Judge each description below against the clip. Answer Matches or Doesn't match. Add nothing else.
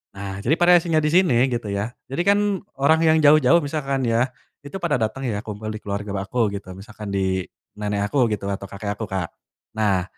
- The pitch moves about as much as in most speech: Doesn't match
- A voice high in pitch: Doesn't match